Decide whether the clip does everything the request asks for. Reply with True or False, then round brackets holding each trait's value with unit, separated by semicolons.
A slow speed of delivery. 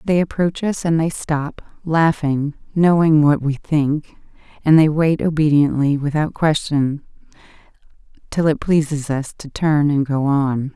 False (145 wpm)